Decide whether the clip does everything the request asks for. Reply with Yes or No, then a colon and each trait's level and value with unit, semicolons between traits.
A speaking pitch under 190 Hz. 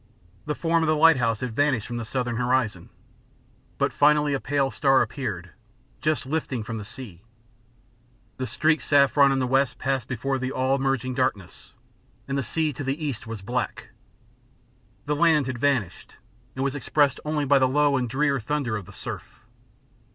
Yes: low, 135 Hz